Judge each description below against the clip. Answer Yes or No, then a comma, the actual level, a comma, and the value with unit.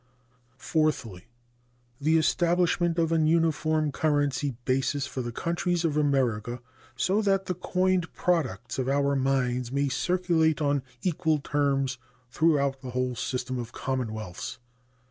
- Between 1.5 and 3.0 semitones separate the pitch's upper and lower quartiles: No, average, 4.3 semitones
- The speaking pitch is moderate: Yes, medium, 145 Hz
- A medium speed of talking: No, slow, 125 wpm